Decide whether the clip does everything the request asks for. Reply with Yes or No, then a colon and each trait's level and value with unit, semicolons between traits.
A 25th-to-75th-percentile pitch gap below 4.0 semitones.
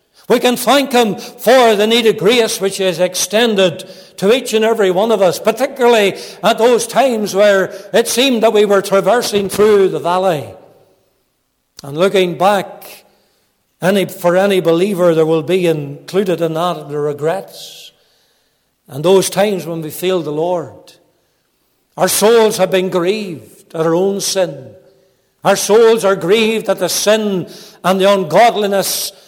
Yes: average, 2.9 semitones